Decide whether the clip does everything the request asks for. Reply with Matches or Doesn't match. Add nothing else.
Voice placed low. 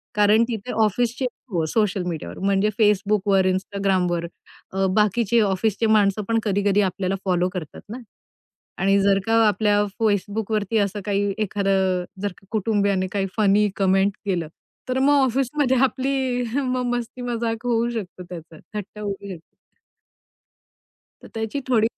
Doesn't match